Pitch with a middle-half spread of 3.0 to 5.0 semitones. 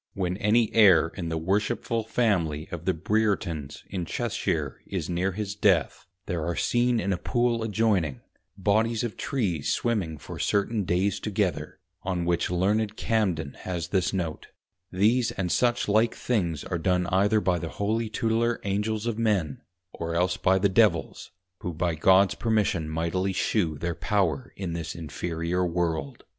Yes: average, 4.2 semitones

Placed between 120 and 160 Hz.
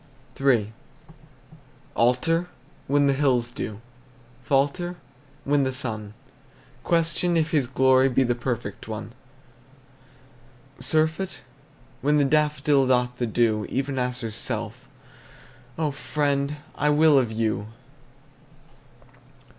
Yes: low, 135 Hz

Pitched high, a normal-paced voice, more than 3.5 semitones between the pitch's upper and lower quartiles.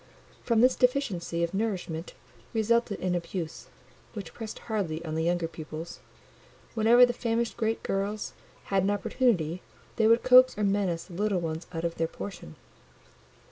Yes: high, 195 Hz; average, 155 wpm; average, 5.1 semitones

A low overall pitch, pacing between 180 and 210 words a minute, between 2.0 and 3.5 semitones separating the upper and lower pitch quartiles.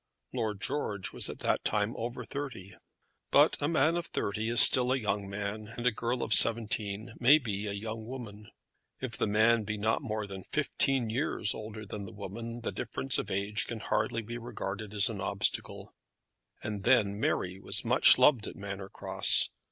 Yes: low, 110 Hz; average, 185 wpm; average, 2.8 semitones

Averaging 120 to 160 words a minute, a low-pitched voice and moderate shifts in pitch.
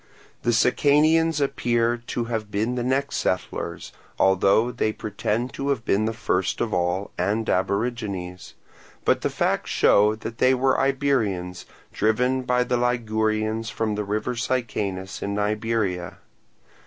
Yes: average, 140 wpm; low, 110 Hz; average, 3.4 semitones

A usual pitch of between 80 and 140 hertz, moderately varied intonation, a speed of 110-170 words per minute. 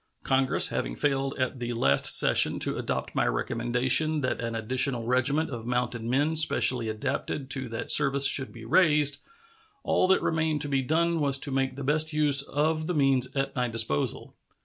No: low, 135 Hz; average, 3.4 semitones; average, 180 wpm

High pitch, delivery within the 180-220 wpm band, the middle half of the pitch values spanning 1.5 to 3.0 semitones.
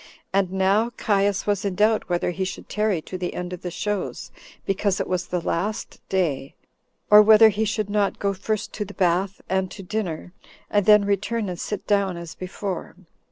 Yes: high, 195 Hz; average, 195 wpm; narrow, 2.4 semitones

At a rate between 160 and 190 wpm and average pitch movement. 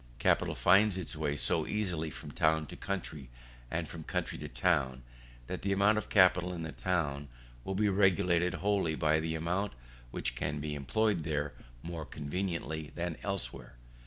Yes: average, 165 wpm; average, 4.3 semitones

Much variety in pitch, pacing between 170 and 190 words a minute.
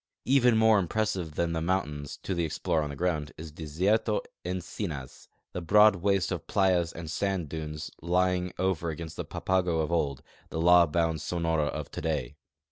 No: average, 2.9 semitones; average, 175 wpm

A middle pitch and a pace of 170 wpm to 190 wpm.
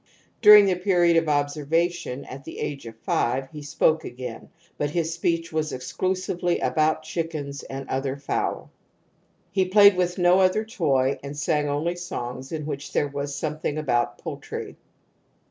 No: medium, 155 Hz; average, 160 wpm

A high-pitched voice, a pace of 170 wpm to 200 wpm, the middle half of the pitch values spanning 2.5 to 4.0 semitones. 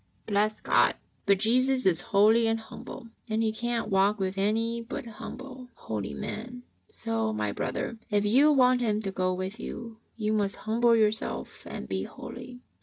Yes: high, 220 Hz; average, 175 wpm; average, 3.1 semitones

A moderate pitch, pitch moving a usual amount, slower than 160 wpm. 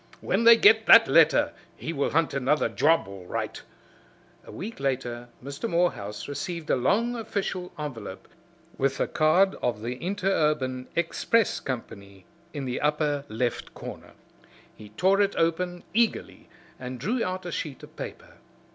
No: medium, 150 Hz; wide, 6.5 semitones; average, 150 wpm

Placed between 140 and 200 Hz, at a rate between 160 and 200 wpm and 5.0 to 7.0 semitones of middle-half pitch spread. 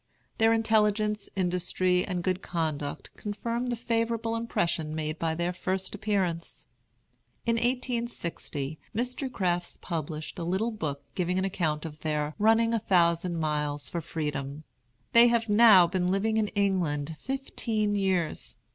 No: medium, 185 Hz; average, 140 wpm; wide, 5.5 semitones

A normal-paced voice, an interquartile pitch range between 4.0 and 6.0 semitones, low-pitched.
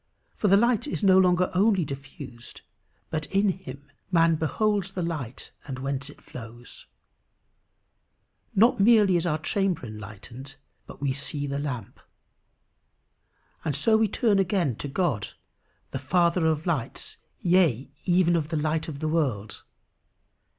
No: average, 145 wpm; wide, 5.4 semitones; medium, 160 Hz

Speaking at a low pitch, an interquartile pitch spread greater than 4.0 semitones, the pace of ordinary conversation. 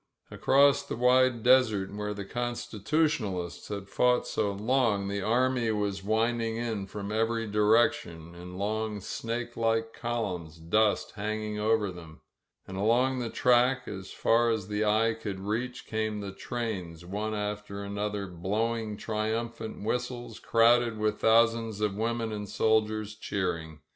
No: low, 110 Hz; narrow, 2.5 semitones; average, 145 wpm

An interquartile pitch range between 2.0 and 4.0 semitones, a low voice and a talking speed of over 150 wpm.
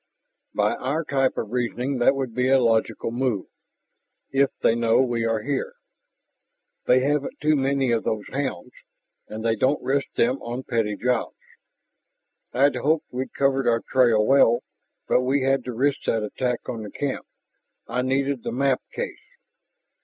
Yes: average, 2.8 semitones; low, 130 Hz; average, 160 wpm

